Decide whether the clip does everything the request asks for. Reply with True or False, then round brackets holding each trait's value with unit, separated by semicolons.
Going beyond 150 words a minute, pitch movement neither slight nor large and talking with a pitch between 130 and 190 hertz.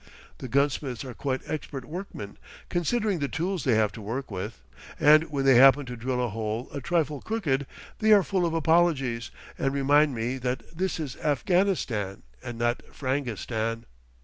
True (170 wpm; 5.0 semitones; 135 Hz)